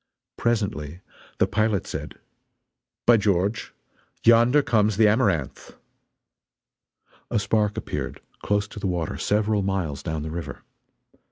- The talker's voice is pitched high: No, low, 105 Hz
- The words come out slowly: Yes, slow, 115 wpm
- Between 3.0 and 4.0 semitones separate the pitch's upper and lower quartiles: Yes, average, 3.7 semitones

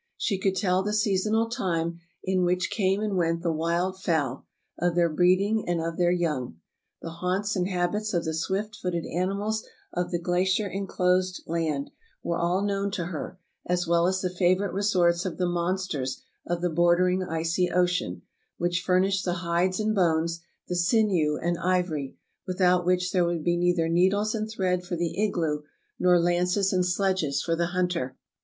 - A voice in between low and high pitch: Yes, medium, 180 Hz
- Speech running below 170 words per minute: No, average, 175 wpm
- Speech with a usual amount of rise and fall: No, narrow, 1.9 semitones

